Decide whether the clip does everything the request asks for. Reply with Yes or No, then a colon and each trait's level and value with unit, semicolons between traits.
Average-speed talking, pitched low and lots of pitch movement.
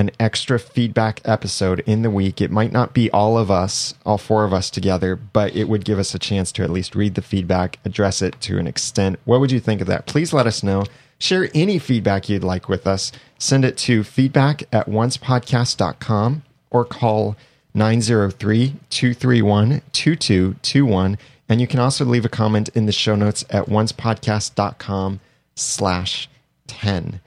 No: average, 170 wpm; low, 110 Hz; average, 3.9 semitones